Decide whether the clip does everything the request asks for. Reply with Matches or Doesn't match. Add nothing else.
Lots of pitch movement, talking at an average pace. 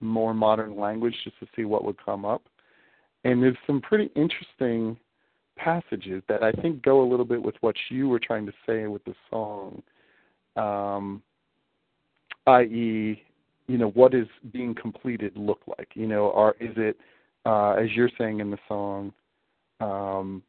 Doesn't match